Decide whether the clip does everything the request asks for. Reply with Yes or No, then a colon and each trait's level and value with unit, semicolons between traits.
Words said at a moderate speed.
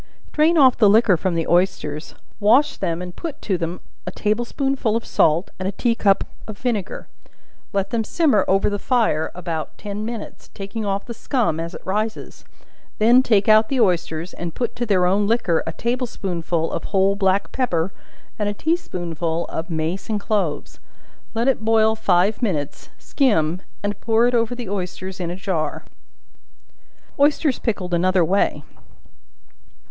Yes: average, 170 wpm